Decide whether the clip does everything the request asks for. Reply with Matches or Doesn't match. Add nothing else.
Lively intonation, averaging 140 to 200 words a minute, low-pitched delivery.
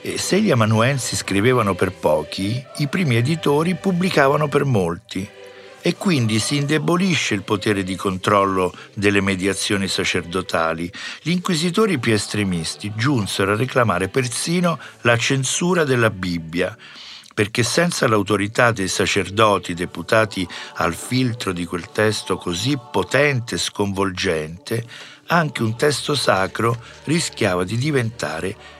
Doesn't match